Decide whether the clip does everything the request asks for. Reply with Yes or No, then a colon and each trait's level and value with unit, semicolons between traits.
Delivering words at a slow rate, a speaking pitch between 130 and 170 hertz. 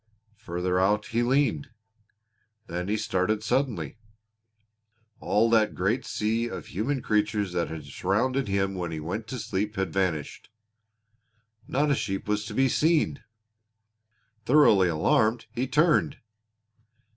No: slow, 130 wpm; low, 105 Hz